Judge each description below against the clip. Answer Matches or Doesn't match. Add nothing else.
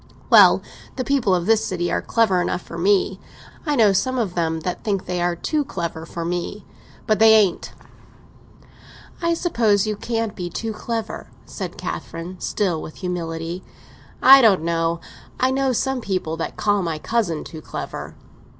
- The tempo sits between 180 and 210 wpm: Doesn't match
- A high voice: Matches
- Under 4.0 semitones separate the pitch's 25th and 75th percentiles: Doesn't match